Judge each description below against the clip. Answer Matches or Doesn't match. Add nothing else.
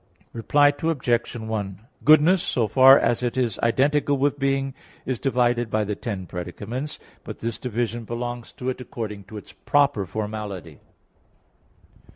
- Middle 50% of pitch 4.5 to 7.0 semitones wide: Doesn't match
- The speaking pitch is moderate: Doesn't match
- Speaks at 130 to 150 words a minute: Matches